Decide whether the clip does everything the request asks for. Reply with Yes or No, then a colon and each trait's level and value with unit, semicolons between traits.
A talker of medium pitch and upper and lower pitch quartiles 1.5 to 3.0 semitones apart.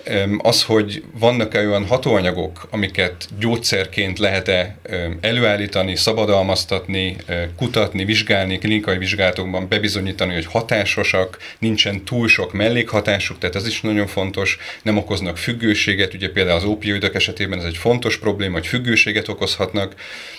No: low, 100 Hz; narrow, 2.6 semitones